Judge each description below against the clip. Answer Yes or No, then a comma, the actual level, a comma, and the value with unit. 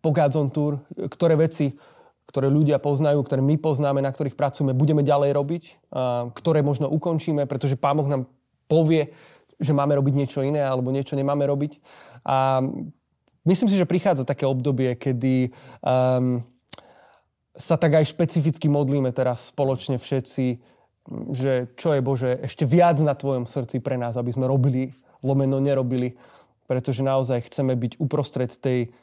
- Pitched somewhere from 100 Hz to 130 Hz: No, medium, 140 Hz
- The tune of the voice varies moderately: No, narrow, 2.3 semitones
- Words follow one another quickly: No, average, 145 wpm